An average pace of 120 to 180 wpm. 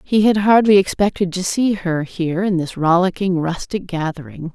Yes: average, 170 wpm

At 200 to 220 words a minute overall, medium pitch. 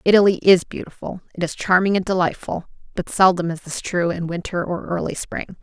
No: average, 190 wpm; medium, 180 Hz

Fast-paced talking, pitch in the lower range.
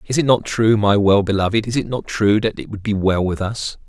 Yes: fast, 280 wpm; low, 105 Hz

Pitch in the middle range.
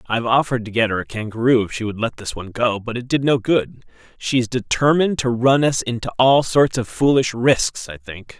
No: low, 120 Hz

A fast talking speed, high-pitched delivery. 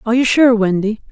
Yes: fast, 215 wpm; high, 230 Hz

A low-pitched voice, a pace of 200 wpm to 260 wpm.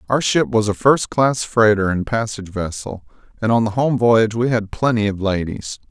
Yes: low, 110 Hz; fast, 205 wpm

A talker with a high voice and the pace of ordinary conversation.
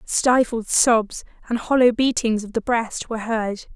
Yes: high, 230 Hz; average, 160 wpm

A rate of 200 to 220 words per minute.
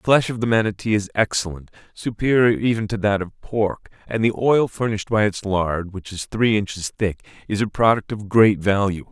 Yes: fast, 205 wpm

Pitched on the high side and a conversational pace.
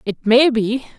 Yes: high, 235 Hz; average, 185 wpm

